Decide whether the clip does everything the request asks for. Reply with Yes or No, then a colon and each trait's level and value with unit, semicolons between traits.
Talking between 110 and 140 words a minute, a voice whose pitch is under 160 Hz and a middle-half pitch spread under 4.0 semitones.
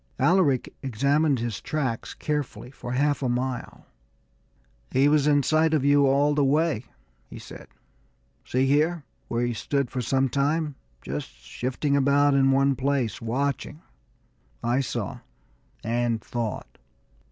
Yes: slow, 135 wpm; low, 135 Hz; average, 2.9 semitones